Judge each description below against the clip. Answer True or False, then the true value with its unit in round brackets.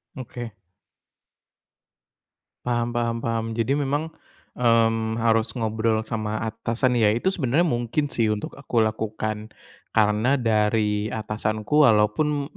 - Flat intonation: True (2.1 semitones)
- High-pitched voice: False (115 Hz)